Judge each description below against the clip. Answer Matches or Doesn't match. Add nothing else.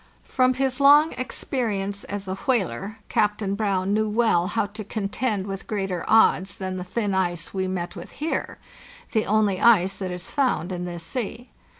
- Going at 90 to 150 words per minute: Doesn't match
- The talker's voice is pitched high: Matches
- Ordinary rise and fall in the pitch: Matches